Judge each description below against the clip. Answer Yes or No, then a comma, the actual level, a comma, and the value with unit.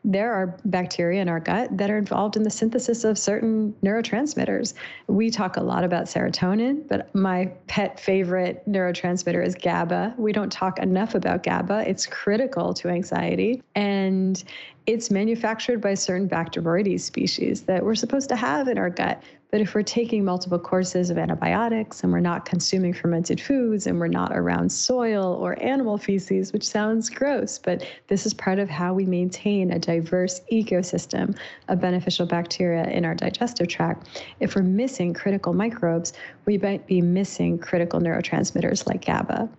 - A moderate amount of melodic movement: Yes, average, 3.3 semitones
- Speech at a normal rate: Yes, average, 165 wpm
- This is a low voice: No, high, 195 Hz